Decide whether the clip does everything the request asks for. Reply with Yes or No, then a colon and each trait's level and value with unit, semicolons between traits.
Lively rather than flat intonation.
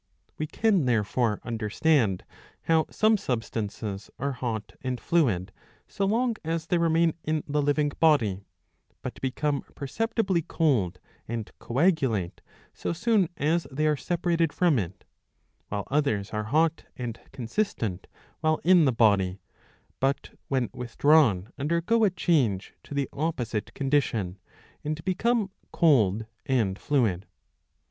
Yes: wide, 6.9 semitones